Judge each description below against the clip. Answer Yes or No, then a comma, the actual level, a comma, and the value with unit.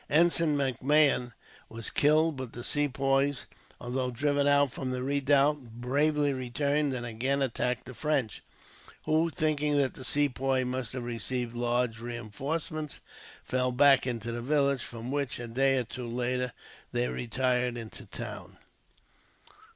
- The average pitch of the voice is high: No, low, 130 Hz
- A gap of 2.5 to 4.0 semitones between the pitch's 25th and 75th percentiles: Yes, average, 2.9 semitones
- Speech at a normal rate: Yes, average, 145 wpm